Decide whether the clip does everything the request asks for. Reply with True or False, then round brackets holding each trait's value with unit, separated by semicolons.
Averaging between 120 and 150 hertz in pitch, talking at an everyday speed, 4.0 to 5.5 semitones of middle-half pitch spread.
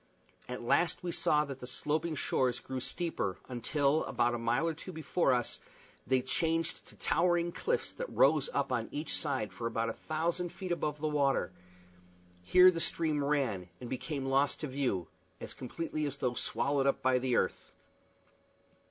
True (140 Hz; 175 wpm; 4.6 semitones)